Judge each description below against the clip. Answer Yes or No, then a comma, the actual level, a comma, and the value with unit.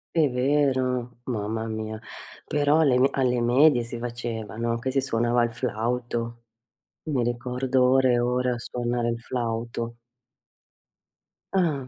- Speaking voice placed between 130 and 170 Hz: No, low, 120 Hz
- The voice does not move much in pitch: Yes, narrow, 1.8 semitones